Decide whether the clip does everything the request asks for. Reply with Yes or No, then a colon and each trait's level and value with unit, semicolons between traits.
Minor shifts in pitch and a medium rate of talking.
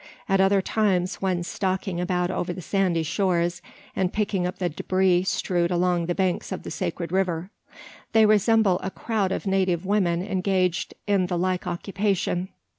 Yes: narrow, 1.6 semitones; average, 165 wpm